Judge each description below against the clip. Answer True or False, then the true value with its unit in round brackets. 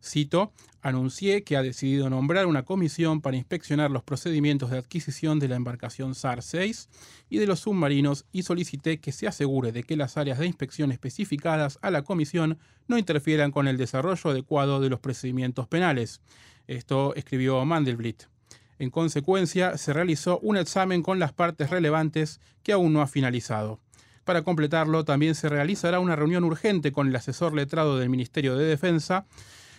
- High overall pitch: False (145 Hz)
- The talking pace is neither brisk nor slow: True (165 wpm)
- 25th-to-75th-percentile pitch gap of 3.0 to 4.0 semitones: False (4.5 semitones)